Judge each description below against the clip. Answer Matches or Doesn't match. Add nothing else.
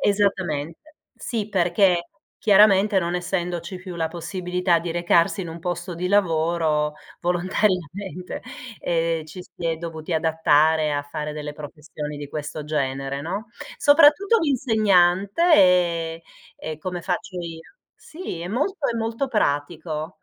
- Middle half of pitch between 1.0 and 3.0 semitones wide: Doesn't match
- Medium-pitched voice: Matches